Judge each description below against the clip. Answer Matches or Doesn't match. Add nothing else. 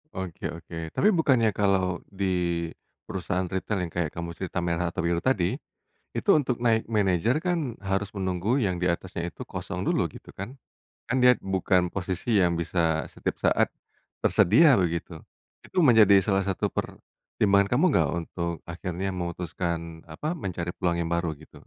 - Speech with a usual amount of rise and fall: Matches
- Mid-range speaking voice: Doesn't match